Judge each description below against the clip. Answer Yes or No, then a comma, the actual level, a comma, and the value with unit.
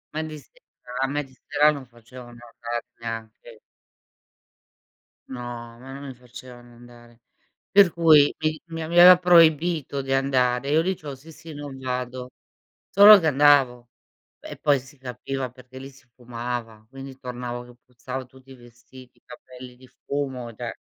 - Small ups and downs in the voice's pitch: No, average, 3.0 semitones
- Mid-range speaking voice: No, low, 130 Hz